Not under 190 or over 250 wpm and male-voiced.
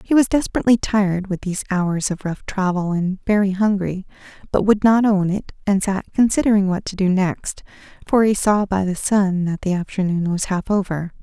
No: average, 200 wpm; female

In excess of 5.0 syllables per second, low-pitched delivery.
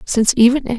No: 7.0 syllables/s; high, 240 Hz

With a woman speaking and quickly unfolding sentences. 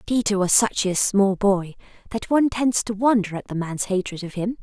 Yes: female; fast, 220 wpm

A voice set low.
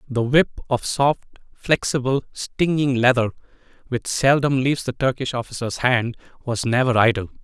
Yes: low, 130 Hz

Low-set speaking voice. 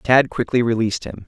Yes: low, 120 Hz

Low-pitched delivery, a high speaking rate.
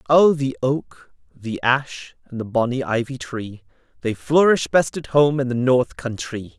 No: low, 130 Hz; average, 175 wpm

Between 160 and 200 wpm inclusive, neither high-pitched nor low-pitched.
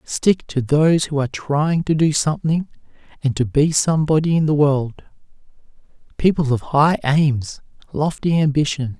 No: average, 140 wpm; medium, 150 Hz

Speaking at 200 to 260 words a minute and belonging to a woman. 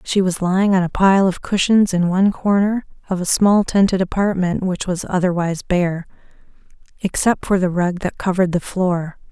No: average, 180 wpm; female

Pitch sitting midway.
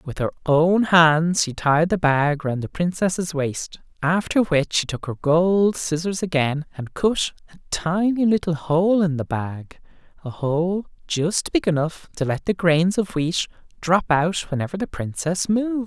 Yes: medium, 170 Hz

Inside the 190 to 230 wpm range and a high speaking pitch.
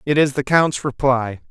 No: average, 200 wpm; low, 135 Hz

